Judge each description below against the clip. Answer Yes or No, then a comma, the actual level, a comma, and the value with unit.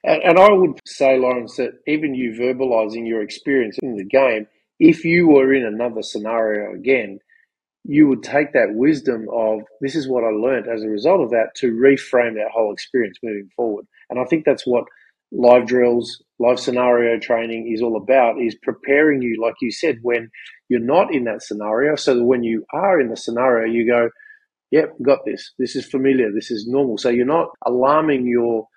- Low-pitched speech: Yes, low, 120 Hz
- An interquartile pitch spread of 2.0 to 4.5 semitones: Yes, average, 3.1 semitones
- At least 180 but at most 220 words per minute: Yes, average, 195 wpm